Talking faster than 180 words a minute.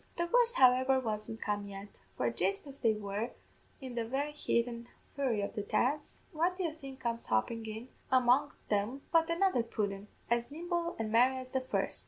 Yes: average, 195 wpm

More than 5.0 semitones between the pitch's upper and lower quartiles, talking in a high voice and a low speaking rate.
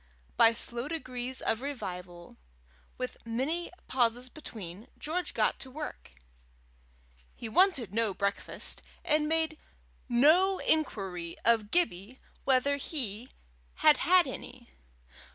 Yes: wide, 5.6 semitones; very high, 255 Hz; slow, 110 wpm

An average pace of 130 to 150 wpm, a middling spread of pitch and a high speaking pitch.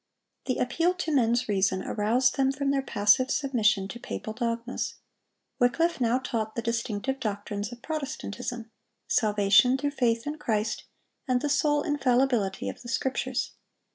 Yes: average, 140 wpm; average, 3.7 semitones; high, 245 Hz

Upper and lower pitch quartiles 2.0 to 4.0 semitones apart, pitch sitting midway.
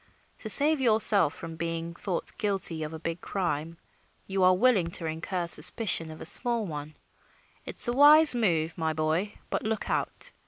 No: average, 5.1 semitones; medium, 180 Hz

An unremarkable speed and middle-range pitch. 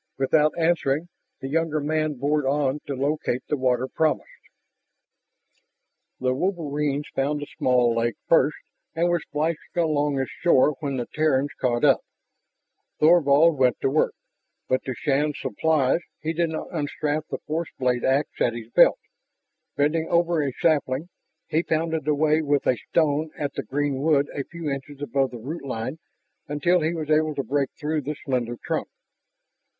Yes: average, 160 wpm; medium, 145 Hz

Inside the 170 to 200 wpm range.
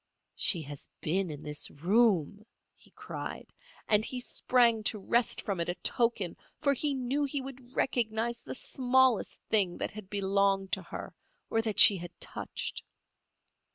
No: average, 155 wpm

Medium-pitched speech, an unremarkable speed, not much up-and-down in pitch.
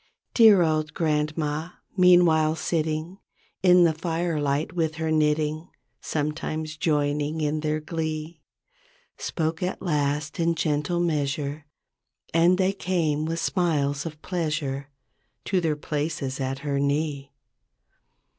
No: medium, 155 Hz; slow, 115 wpm; narrow, 2.0 semitones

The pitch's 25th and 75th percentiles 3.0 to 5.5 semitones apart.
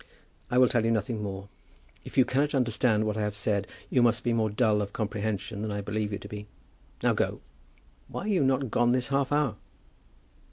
Yes: average, 3.4 semitones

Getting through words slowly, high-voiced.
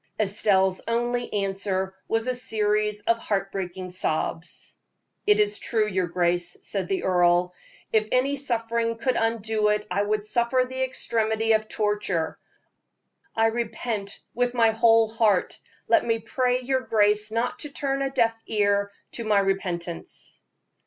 No: average, 145 wpm; high, 215 Hz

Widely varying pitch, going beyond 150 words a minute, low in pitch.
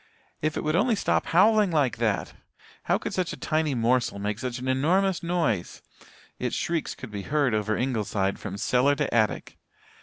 Yes: wide, 7.1 semitones; average, 180 wpm; low, 130 Hz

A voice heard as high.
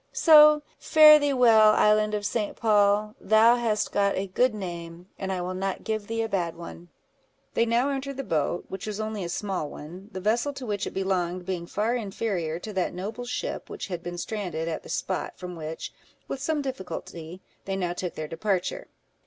Yes: high, 200 Hz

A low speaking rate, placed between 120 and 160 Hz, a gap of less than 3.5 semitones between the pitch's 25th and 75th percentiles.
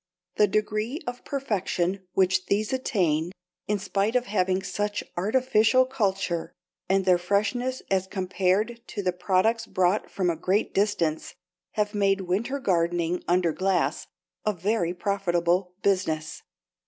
No: slow, 130 wpm; high, 195 Hz; average, 2.9 semitones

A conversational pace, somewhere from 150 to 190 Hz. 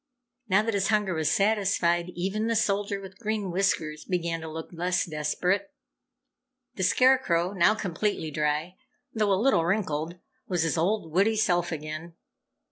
Yes: average, 150 wpm; medium, 185 Hz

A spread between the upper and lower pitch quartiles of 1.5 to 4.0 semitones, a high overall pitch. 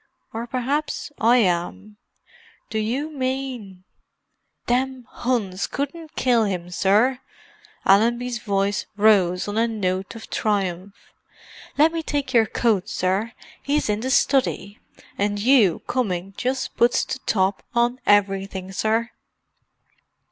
No: average, 4.5 semitones; high, 220 Hz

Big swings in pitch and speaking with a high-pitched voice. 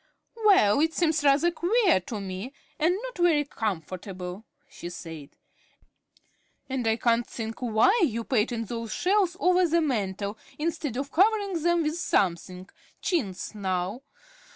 Yes: wide, 9.0 semitones; very high, 250 Hz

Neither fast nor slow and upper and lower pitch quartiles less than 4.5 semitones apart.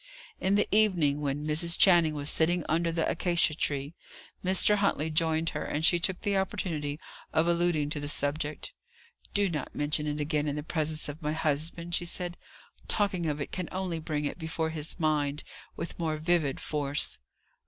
Yes: average, 180 wpm; average, 2.7 semitones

